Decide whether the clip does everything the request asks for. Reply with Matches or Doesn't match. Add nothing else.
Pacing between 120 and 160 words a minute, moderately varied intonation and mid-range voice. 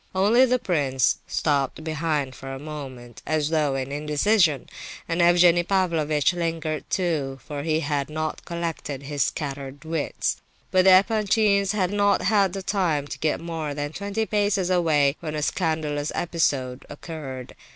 Matches